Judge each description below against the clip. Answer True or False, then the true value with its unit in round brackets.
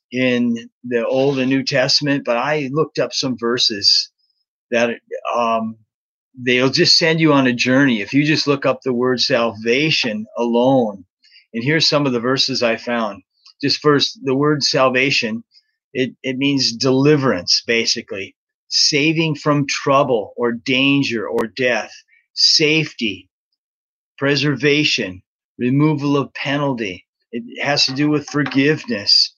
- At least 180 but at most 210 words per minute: False (135 wpm)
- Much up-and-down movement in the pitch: False (3.5 semitones)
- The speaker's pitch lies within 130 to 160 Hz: True (135 Hz)